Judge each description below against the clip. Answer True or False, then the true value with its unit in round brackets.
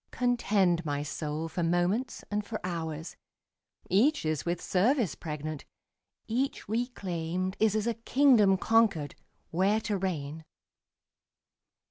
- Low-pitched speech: False (185 Hz)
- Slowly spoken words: True (115 wpm)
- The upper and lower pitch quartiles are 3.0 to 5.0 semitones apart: False (5.5 semitones)